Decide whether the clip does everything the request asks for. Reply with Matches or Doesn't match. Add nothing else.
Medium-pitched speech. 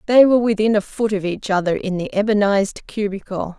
Doesn't match